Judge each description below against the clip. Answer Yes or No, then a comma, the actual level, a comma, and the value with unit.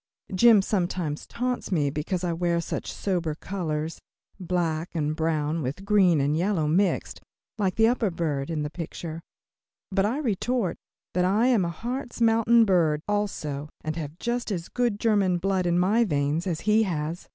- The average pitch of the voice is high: No, medium, 180 Hz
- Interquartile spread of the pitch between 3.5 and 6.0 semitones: Yes, average, 4.8 semitones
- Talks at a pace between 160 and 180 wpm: Yes, average, 170 wpm